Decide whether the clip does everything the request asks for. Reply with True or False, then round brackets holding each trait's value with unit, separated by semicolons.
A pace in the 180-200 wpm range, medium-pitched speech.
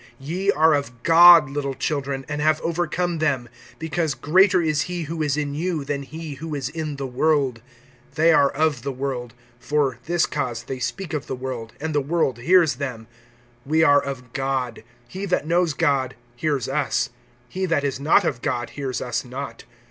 True (185 wpm; 145 Hz)